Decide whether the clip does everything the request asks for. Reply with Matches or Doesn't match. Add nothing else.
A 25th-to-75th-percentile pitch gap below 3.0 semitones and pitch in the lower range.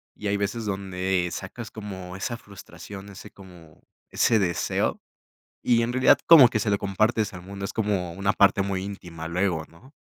Matches